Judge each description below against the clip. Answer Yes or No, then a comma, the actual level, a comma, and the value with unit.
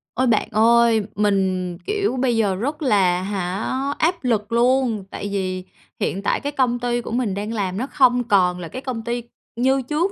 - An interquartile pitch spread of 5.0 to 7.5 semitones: No, average, 4.5 semitones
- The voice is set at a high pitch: Yes, high, 230 Hz